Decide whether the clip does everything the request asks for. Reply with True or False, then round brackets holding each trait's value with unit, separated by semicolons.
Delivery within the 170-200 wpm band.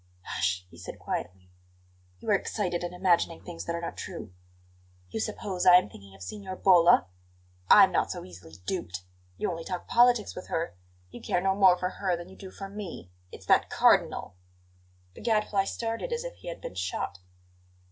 True (190 wpm)